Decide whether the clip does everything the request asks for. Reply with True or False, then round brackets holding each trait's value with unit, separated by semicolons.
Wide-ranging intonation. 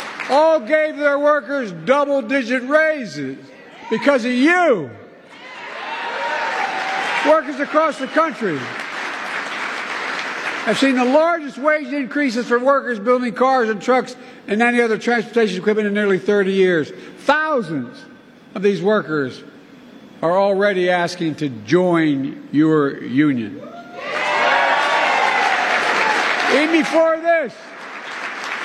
True (6.1 semitones)